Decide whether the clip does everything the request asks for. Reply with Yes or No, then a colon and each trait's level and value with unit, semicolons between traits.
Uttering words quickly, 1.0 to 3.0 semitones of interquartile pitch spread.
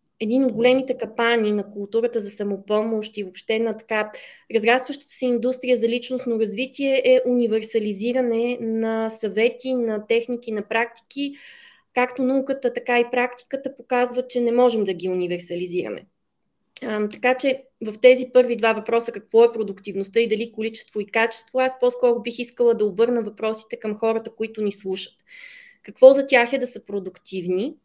No: average, 155 wpm; narrow, 2.6 semitones